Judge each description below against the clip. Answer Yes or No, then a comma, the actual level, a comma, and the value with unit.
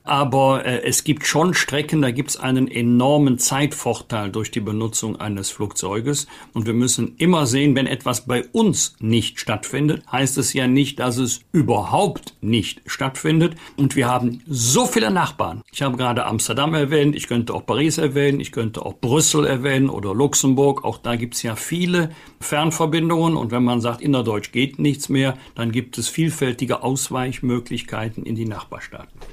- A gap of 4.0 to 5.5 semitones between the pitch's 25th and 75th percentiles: No, average, 3.6 semitones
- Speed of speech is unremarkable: Yes, average, 175 wpm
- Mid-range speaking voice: No, low, 130 Hz